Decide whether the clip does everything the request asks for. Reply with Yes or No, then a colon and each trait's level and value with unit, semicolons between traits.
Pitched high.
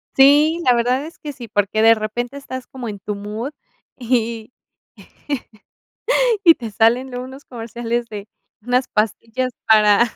Yes: high, 235 Hz